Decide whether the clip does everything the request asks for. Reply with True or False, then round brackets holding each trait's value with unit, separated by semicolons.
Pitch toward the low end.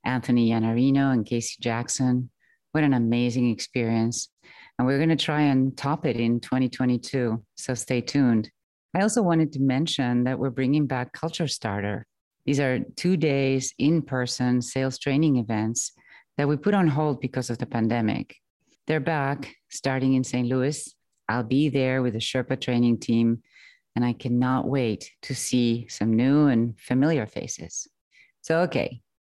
True (130 Hz)